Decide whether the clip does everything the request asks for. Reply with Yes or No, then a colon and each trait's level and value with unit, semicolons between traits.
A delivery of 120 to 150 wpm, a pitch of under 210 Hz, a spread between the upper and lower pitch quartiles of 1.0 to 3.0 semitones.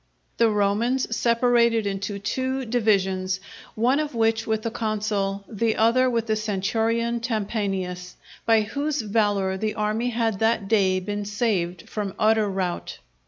No: average, 140 wpm; high, 215 Hz; average, 2.7 semitones